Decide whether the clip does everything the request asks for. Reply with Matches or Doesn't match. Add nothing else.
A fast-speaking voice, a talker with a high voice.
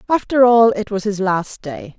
Matches